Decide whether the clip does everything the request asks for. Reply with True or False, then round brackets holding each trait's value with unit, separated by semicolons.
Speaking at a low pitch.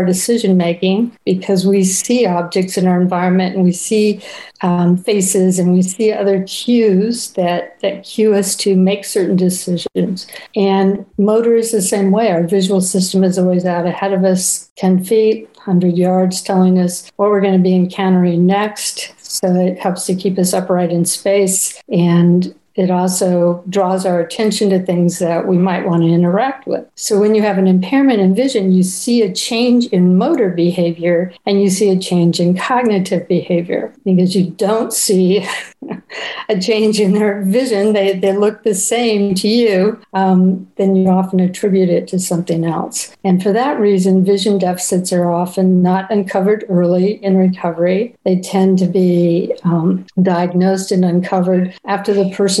False (190 Hz)